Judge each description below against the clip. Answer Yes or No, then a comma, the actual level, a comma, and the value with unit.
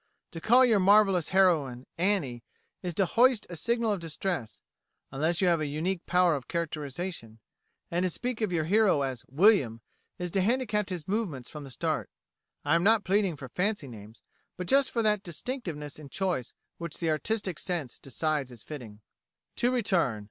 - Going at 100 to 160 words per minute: No, average, 175 wpm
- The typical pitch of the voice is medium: Yes, medium, 175 Hz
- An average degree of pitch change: No, wide, 5.9 semitones